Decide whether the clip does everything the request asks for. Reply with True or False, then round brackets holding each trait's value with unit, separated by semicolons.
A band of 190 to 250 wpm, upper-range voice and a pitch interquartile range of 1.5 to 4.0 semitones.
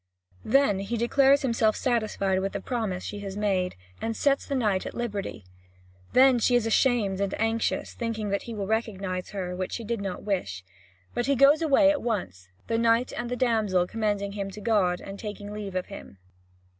True (195 wpm; 215 Hz; 3.4 semitones)